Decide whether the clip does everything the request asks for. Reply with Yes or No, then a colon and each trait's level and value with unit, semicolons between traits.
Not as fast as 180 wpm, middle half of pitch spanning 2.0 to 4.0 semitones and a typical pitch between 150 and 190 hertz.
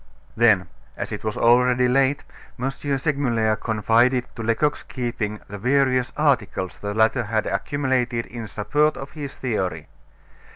No: slow, 135 wpm; average, 3.6 semitones; low, 120 Hz